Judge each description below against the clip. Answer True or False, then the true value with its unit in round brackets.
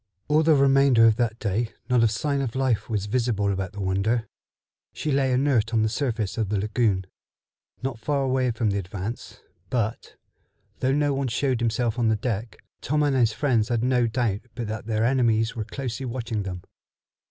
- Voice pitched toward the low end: True (115 Hz)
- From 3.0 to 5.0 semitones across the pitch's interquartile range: True (3.3 semitones)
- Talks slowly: False (190 wpm)